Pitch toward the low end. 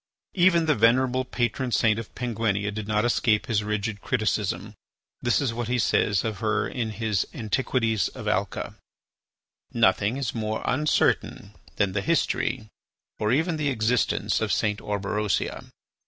Yes: low, 110 Hz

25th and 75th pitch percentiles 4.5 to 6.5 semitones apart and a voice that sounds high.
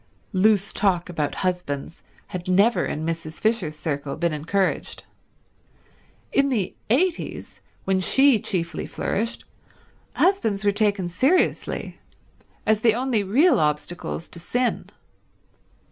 Yes: average, 5.2 semitones; high, 195 Hz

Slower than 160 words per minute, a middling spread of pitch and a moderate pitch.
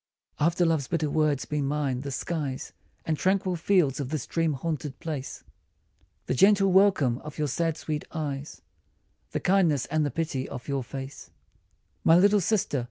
No: average, 165 wpm; average, 3.6 semitones; medium, 155 Hz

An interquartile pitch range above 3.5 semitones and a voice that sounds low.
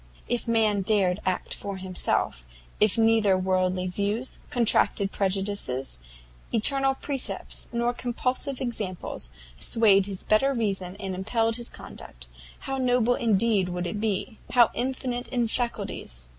No: average, 4.2 semitones; high, 215 Hz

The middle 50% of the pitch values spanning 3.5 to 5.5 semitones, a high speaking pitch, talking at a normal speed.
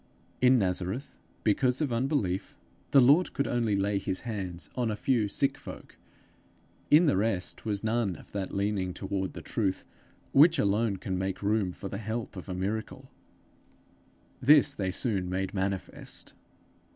No: average, 4.3 semitones; low, 105 Hz; average, 155 wpm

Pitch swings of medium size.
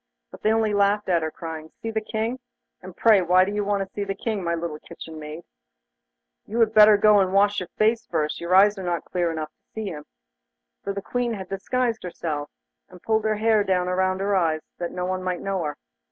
Yes: average, 3.7 semitones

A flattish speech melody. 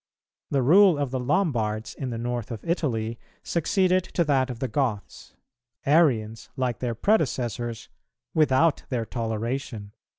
No: average, 4.8 semitones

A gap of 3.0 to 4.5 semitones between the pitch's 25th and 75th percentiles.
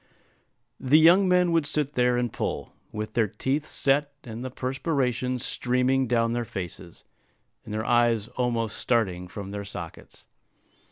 Yes: average, 3.6 semitones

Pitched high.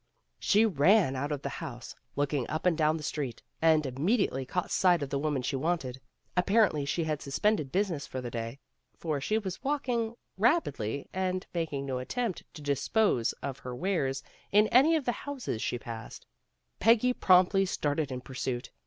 No: medium, 155 Hz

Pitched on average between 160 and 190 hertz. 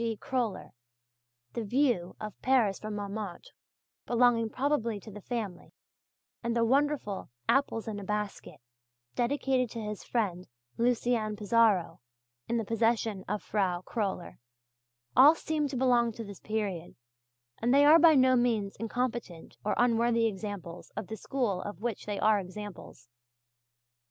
No: high, 225 Hz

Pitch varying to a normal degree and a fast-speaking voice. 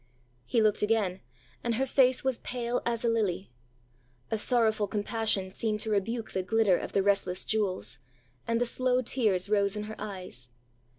No: average, 3.0 semitones; average, 175 wpm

